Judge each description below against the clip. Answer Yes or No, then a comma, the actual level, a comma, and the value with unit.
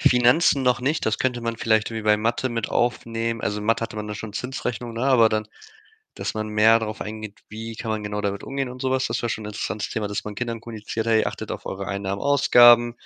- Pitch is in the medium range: No, low, 115 Hz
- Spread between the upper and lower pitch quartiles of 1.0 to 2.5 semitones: Yes, narrow, 2.2 semitones